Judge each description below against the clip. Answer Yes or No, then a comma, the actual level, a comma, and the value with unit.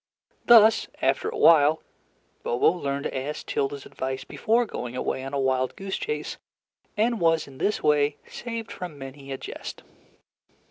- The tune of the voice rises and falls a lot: Yes, wide, 7.8 semitones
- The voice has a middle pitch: Yes, medium, 150 Hz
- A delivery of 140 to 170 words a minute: Yes, average, 155 wpm